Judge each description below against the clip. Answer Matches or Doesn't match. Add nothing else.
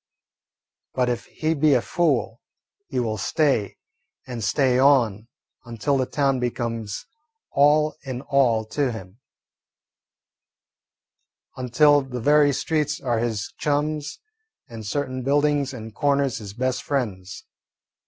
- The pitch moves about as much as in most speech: Matches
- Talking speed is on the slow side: Matches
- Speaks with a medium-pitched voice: Doesn't match